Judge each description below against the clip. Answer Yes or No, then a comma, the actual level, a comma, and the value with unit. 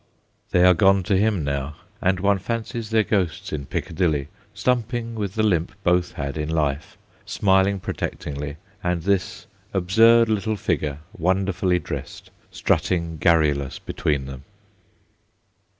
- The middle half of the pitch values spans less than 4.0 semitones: No, average, 4.9 semitones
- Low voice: Yes, very low, 90 Hz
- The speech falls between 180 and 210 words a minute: No, slow, 135 wpm